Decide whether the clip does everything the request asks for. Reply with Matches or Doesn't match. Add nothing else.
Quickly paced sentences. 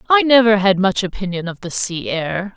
Matches